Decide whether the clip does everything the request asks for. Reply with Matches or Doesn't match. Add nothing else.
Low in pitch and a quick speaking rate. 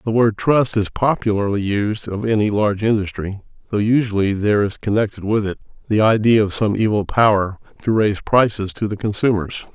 Doesn't match